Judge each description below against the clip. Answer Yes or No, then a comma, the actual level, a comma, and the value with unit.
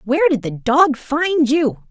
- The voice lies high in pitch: Yes, very high, 275 Hz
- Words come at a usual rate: Yes, average, 190 wpm